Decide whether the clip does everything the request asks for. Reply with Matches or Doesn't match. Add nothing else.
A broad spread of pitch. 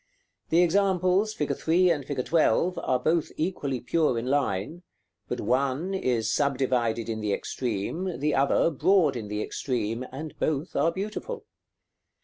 Matches